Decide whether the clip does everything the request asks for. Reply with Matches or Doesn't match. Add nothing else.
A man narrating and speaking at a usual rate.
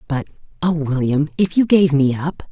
Doesn't match